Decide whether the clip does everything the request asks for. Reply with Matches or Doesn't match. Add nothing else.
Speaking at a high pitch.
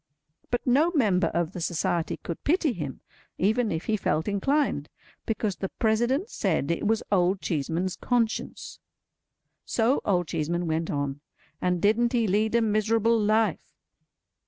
Matches